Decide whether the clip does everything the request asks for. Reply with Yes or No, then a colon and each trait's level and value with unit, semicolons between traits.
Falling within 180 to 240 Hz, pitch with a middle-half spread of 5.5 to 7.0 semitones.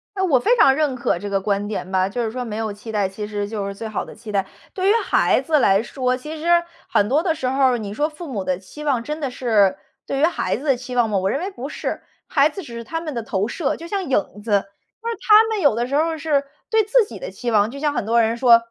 No: very high, 250 Hz; wide, 6.6 semitones